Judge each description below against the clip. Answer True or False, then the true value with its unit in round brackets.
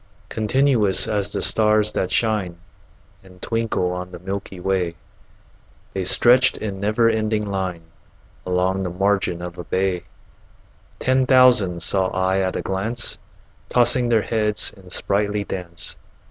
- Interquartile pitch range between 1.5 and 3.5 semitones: True (3.2 semitones)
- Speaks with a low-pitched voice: True (100 Hz)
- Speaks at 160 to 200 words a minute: False (135 wpm)